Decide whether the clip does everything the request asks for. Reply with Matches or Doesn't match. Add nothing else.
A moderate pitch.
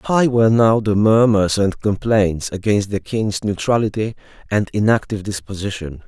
Doesn't match